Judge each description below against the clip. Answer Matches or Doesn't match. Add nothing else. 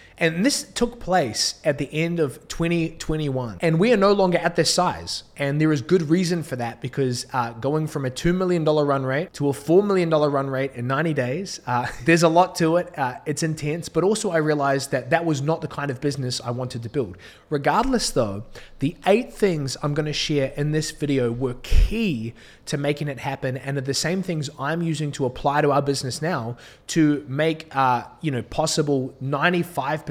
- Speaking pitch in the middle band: Matches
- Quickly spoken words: Matches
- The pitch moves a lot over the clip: Doesn't match